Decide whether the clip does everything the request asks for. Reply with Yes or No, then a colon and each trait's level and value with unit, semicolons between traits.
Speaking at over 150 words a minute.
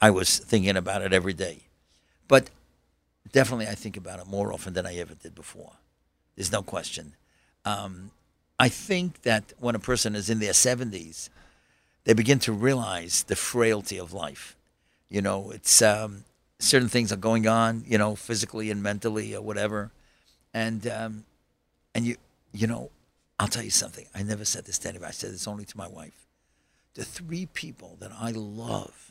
Yes: average, 180 wpm